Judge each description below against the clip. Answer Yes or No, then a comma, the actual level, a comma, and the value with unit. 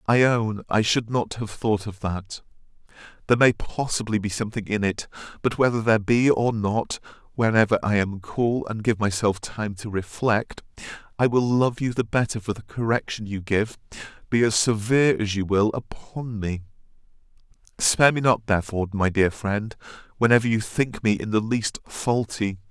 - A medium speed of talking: Yes, average, 175 wpm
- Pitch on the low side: Yes, low, 110 Hz